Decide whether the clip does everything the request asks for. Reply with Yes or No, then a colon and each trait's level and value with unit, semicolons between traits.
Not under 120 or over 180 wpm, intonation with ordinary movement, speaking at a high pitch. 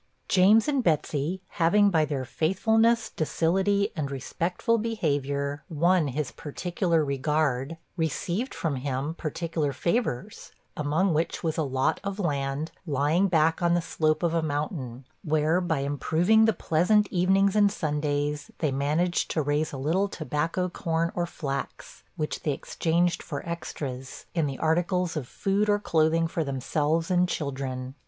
No: average, 145 wpm; average, 3.8 semitones; medium, 160 Hz